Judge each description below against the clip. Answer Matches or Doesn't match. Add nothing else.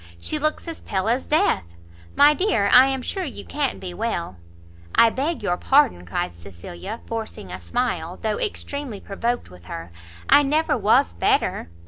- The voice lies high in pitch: Matches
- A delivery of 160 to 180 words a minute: Matches